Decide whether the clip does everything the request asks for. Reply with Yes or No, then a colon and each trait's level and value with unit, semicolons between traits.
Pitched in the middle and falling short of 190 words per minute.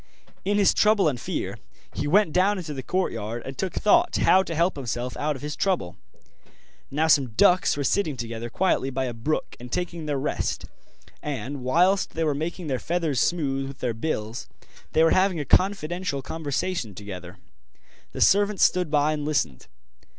Yes: medium, 150 Hz; average, 180 wpm